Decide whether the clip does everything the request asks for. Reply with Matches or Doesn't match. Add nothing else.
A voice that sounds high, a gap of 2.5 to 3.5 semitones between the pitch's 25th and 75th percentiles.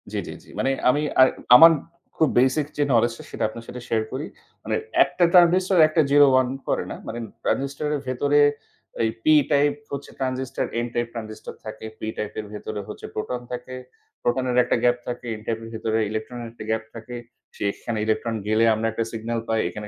Doesn't match